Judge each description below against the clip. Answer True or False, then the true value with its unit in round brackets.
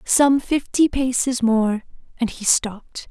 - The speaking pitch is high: True (245 Hz)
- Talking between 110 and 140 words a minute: True (135 wpm)